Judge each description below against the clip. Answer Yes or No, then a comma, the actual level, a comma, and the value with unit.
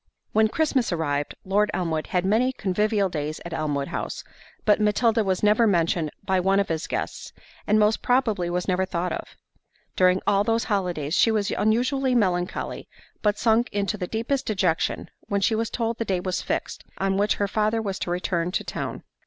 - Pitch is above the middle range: Yes, high, 200 Hz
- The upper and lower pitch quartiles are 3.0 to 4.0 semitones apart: Yes, average, 3.5 semitones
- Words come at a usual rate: Yes, average, 185 wpm